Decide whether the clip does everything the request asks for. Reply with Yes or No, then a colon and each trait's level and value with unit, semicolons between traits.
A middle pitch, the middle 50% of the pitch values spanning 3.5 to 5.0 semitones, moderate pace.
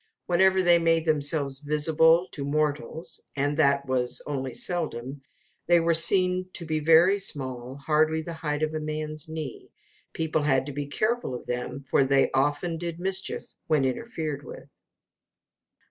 No: medium, 155 Hz; average, 3.0 semitones; average, 155 wpm